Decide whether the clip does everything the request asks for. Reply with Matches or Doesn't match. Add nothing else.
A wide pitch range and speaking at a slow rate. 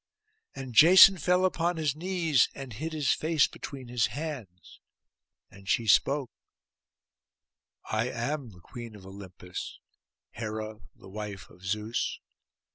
Matches